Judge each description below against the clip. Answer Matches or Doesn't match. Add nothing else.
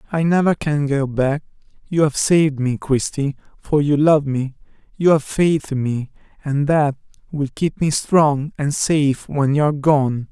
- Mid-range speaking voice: Matches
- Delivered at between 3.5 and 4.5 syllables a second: Matches